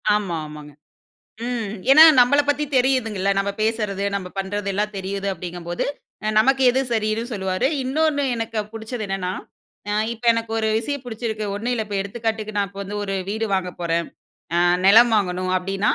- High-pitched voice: Yes, high, 210 Hz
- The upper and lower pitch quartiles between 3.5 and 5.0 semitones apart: No, average, 3.1 semitones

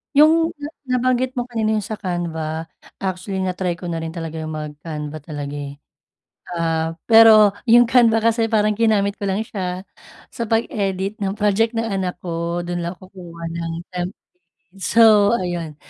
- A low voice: No, high, 190 Hz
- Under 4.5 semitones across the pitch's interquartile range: No, average, 4.8 semitones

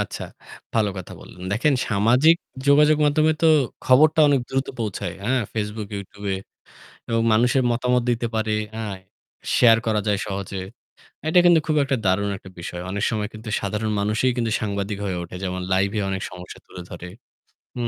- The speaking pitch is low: Yes, low, 110 Hz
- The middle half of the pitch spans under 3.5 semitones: No, average, 4.2 semitones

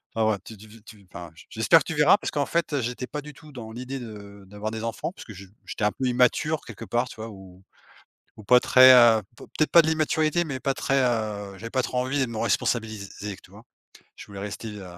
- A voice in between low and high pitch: No, low, 115 Hz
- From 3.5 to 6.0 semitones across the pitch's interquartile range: Yes, average, 3.8 semitones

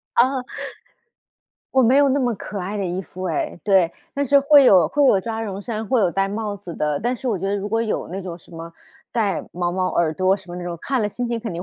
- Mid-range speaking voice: No, high, 205 Hz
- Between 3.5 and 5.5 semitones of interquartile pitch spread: Yes, average, 4.8 semitones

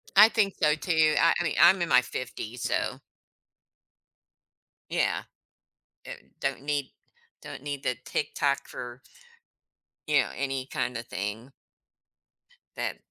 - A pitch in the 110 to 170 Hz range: Yes, medium, 140 Hz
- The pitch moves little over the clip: No, average, 3.6 semitones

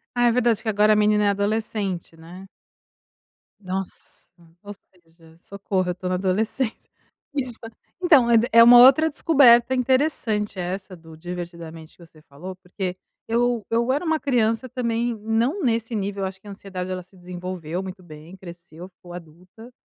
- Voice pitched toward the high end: Yes, high, 200 Hz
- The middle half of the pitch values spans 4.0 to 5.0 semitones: Yes, average, 4.6 semitones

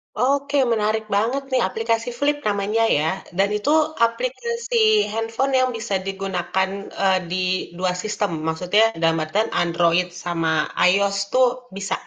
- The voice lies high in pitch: Yes, high, 210 Hz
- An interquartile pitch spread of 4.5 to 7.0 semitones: Yes, average, 4.8 semitones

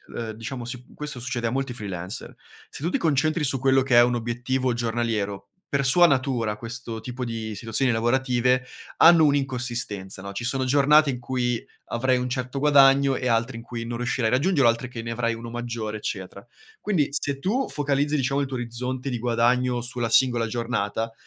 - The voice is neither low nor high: No, low, 125 Hz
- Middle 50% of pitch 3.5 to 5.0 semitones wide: No, narrow, 2.6 semitones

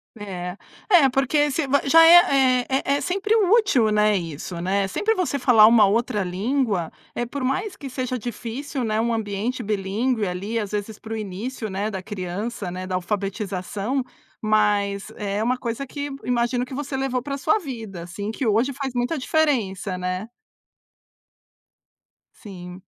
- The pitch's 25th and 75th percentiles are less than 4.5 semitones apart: No, average, 5.1 semitones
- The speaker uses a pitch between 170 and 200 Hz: No, high, 225 Hz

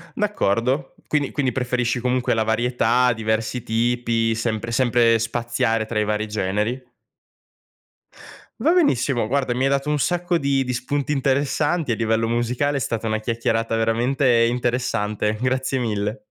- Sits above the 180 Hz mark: No, low, 120 Hz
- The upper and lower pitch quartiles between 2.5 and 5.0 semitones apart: Yes, average, 2.9 semitones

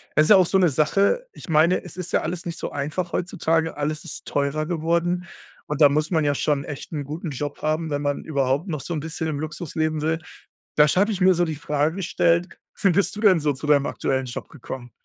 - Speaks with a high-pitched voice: No, medium, 155 Hz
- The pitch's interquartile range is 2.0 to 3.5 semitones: Yes, average, 3.0 semitones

